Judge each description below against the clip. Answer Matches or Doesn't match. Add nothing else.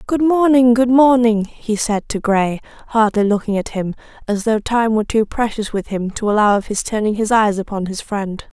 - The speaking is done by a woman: Matches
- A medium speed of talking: Doesn't match